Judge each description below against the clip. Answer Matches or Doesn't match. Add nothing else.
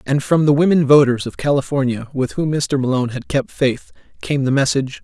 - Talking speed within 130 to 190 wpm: Doesn't match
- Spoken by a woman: Doesn't match